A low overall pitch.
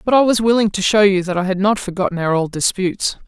No: high, 195 Hz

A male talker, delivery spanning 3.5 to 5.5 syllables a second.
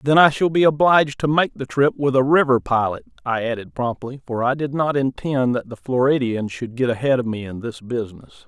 Yes: male; 5.4 syllables/s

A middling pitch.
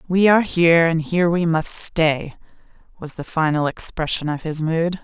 Yes: medium, 165 Hz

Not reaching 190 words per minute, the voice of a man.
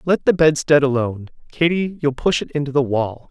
No: average, 200 wpm; male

